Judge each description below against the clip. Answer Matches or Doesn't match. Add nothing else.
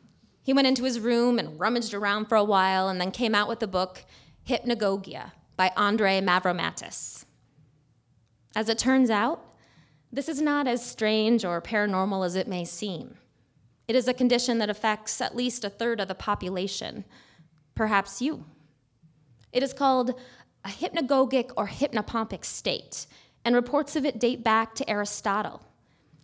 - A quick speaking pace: Doesn't match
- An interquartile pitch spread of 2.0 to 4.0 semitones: Doesn't match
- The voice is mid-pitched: Doesn't match